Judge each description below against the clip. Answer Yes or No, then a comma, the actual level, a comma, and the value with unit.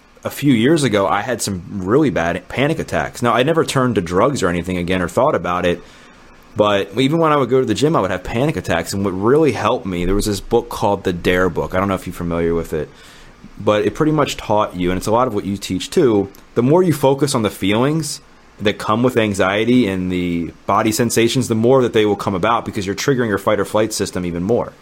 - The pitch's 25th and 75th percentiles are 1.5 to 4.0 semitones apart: No, average, 5.1 semitones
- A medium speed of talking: No, fast, 255 wpm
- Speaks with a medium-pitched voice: No, low, 105 Hz